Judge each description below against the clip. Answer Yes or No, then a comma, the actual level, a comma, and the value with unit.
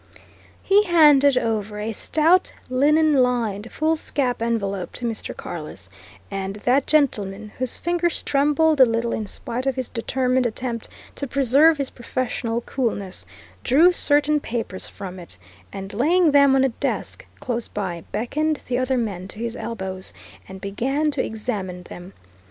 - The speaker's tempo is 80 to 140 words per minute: No, average, 150 wpm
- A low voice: No, high, 245 Hz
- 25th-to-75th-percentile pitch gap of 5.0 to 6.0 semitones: Yes, average, 5.3 semitones